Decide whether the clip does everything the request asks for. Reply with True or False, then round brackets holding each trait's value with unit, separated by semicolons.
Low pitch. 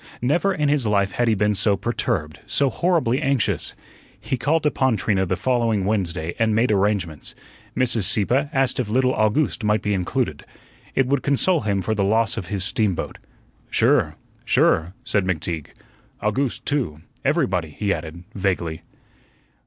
True (110 Hz)